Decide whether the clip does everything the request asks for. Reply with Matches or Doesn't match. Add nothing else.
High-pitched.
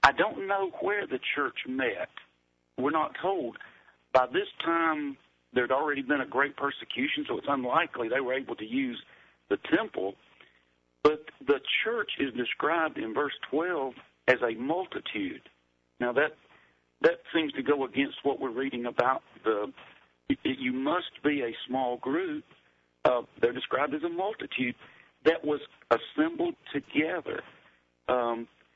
Doesn't match